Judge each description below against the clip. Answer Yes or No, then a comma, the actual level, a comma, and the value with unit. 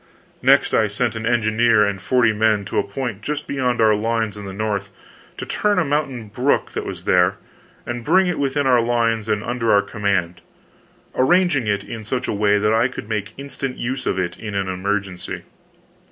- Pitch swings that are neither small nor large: Yes, average, 3.7 semitones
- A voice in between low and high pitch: No, low, 110 Hz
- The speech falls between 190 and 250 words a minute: Yes, average, 195 wpm